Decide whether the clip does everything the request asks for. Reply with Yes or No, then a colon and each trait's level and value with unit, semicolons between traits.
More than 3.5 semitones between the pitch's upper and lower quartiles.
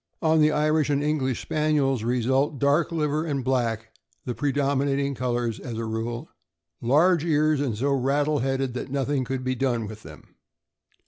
No: average, 3.2 semitones